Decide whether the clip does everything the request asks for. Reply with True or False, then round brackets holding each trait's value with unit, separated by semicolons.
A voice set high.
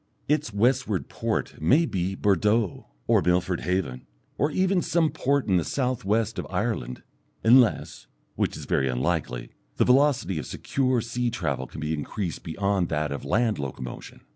False (100 Hz)